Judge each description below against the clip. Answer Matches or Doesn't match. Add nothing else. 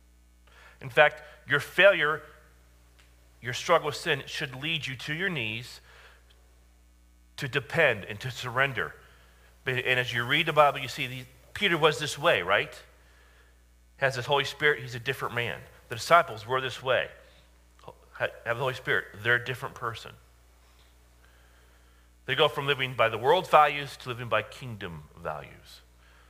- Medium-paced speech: Matches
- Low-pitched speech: Matches